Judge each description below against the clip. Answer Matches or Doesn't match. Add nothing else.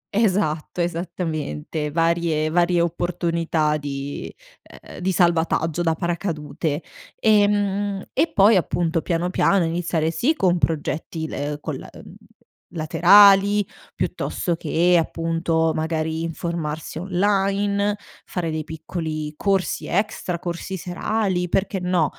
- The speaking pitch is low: Doesn't match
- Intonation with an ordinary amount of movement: Matches